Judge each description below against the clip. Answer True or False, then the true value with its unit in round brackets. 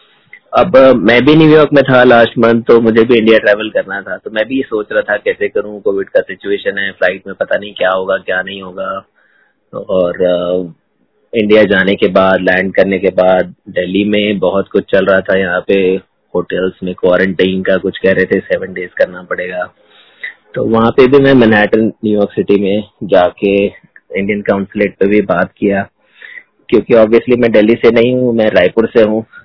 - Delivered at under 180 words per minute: False (190 wpm)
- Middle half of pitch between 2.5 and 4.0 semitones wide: True (3.6 semitones)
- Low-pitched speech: True (105 Hz)